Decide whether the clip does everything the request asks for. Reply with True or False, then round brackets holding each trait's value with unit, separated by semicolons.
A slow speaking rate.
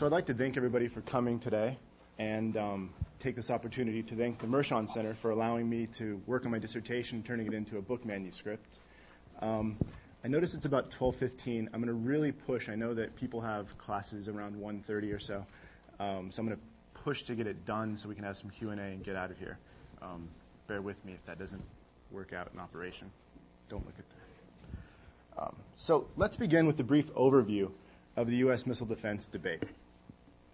False (205 wpm)